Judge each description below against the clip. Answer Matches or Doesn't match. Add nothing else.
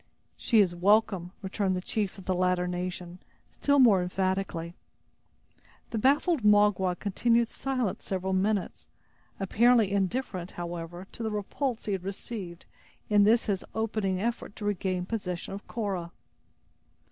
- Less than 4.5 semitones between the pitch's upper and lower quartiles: Matches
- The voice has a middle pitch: Doesn't match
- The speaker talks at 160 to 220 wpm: Doesn't match